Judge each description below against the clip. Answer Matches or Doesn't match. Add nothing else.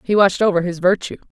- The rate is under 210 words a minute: Doesn't match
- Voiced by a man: Doesn't match